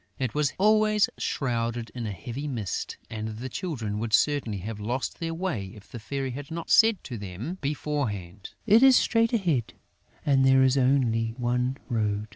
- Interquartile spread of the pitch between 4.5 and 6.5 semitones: Yes, average, 5.2 semitones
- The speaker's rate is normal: Yes, average, 175 wpm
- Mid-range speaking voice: No, low, 125 Hz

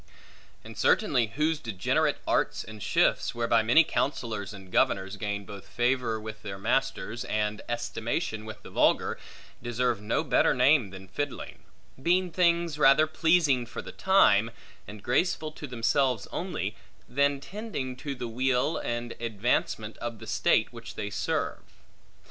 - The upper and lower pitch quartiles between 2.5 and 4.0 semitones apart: No, average, 4.9 semitones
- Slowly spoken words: No, average, 145 wpm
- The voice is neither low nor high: No, low, 120 Hz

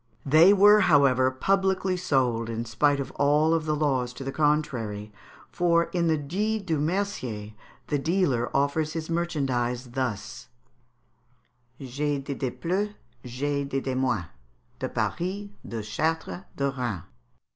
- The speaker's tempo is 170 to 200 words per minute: No, slow, 135 wpm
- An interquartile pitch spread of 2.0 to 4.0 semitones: No, average, 4.8 semitones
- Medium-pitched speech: Yes, medium, 145 Hz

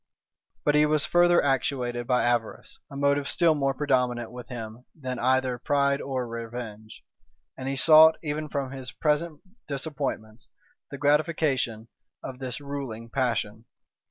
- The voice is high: No, low, 135 Hz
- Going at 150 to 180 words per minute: No, average, 140 wpm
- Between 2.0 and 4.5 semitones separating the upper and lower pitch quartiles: Yes, average, 3.2 semitones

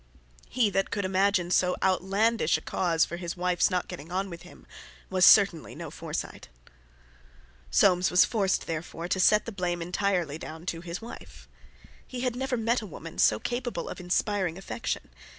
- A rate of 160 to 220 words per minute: Yes, average, 170 wpm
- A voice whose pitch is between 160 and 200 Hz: Yes, medium, 185 Hz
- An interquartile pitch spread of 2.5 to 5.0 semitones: Yes, average, 3.1 semitones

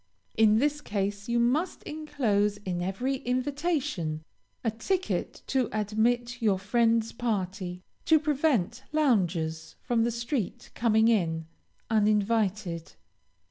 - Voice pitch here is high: Yes, high, 225 Hz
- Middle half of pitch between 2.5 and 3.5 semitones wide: No, average, 4.4 semitones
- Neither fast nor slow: No, slow, 110 wpm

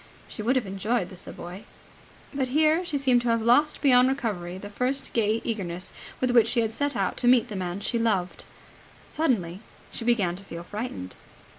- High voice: Yes, high, 230 Hz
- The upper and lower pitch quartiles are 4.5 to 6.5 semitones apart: Yes, average, 4.8 semitones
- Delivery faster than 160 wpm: Yes, average, 190 wpm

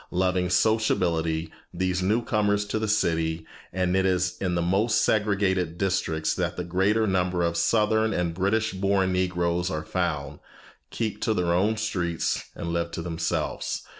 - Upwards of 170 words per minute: No, average, 160 wpm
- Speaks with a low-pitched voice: Yes, very low, 90 Hz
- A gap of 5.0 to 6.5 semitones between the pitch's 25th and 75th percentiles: No, average, 3.2 semitones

